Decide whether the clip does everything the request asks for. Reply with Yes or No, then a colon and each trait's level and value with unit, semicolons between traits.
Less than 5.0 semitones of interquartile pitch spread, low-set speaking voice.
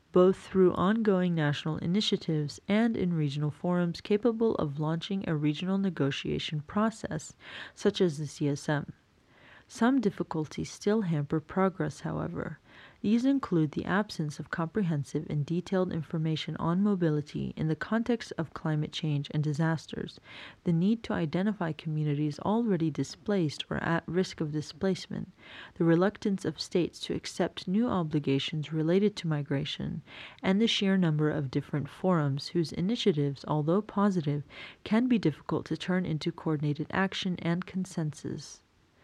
No: average, 4.2 semitones; medium, 170 Hz